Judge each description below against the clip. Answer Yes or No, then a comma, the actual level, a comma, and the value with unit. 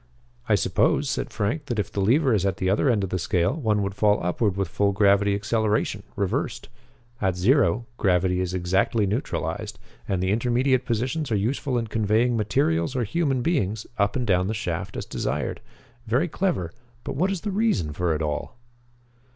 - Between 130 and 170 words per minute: No, average, 185 wpm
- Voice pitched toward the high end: No, low, 105 Hz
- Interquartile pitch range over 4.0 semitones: Yes, average, 4.7 semitones